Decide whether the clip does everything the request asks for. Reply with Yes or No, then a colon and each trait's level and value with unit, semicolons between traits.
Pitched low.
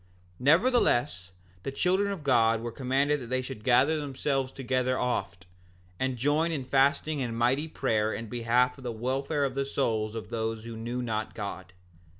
Yes: low, 130 Hz